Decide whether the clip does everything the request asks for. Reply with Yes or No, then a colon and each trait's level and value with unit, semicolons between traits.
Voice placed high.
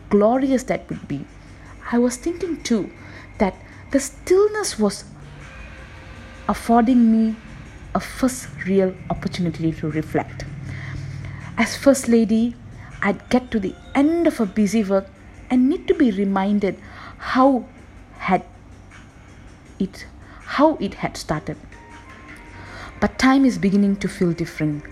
Yes: high, 200 Hz